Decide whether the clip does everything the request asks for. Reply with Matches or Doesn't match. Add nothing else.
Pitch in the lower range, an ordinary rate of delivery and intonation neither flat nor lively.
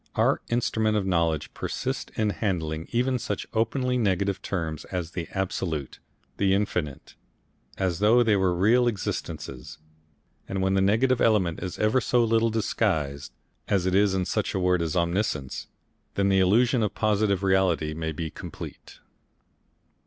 Matches